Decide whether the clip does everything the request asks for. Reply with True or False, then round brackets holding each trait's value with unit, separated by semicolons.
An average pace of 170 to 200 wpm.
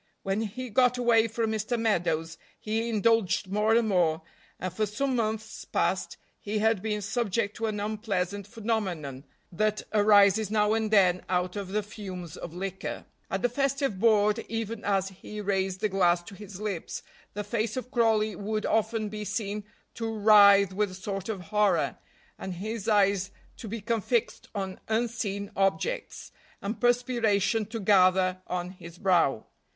False (160 wpm)